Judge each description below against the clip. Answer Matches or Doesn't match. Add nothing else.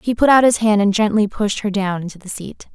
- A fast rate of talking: Matches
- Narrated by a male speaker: Doesn't match